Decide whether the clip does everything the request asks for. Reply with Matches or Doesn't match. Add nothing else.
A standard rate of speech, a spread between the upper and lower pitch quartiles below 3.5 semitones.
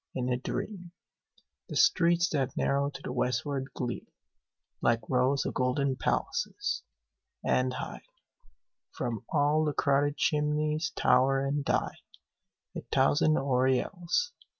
Doesn't match